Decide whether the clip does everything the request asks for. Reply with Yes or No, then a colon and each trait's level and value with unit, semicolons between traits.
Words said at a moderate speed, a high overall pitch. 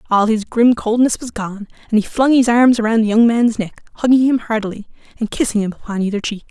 No: fast, 230 wpm; high, 225 Hz